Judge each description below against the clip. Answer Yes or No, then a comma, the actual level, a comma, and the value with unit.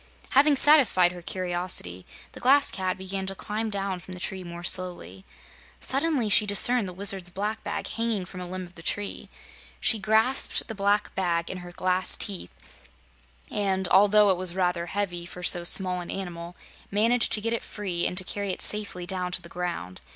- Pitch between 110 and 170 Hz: No, high, 190 Hz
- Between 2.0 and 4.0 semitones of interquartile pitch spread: Yes, average, 2.7 semitones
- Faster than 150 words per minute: Yes, average, 190 wpm